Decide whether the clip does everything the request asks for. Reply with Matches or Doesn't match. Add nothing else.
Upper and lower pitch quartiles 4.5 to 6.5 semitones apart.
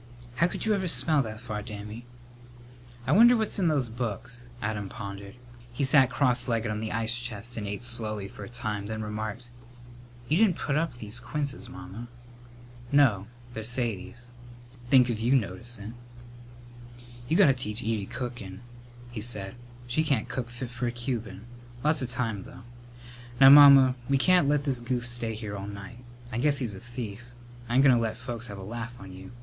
Doesn't match